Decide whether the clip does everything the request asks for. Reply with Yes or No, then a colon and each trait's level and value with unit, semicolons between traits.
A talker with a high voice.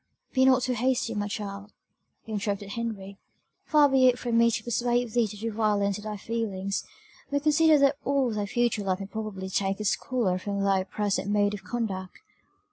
Yes: high, 215 Hz